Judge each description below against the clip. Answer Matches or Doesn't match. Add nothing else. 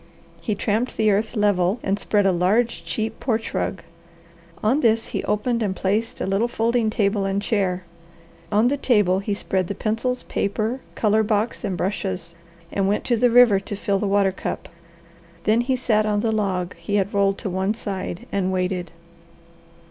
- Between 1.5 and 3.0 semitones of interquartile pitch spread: Matches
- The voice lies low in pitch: Doesn't match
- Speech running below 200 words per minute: Matches